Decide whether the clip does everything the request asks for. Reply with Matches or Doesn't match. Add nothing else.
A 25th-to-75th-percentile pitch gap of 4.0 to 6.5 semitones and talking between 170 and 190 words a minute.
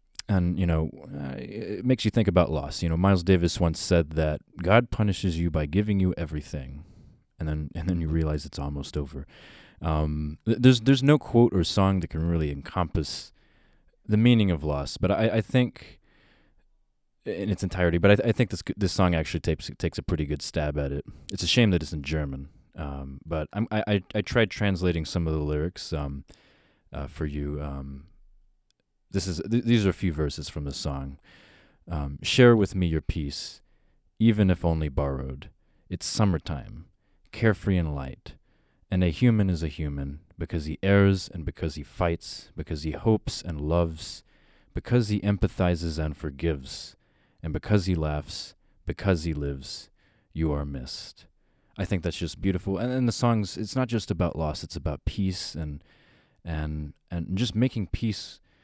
Matches